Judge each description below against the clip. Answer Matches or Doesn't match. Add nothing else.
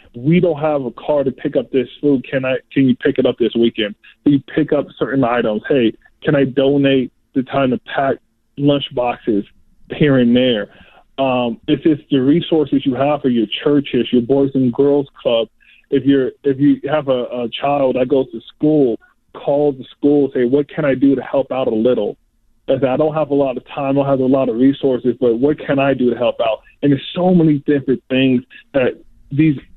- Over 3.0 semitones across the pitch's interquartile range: Doesn't match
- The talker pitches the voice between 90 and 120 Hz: Doesn't match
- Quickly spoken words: Matches